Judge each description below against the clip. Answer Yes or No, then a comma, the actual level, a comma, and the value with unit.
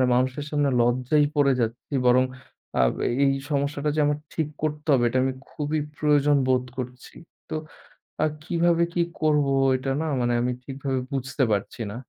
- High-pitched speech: No, medium, 140 Hz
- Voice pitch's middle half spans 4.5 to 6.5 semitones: No, average, 2.7 semitones